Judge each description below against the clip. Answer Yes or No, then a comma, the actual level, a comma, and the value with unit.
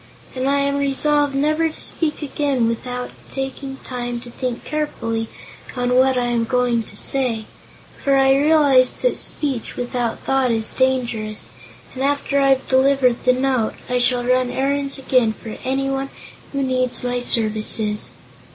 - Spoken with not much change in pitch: Yes, narrow, 2.1 semitones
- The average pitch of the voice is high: Yes, very high, 260 Hz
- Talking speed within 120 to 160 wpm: Yes, average, 150 wpm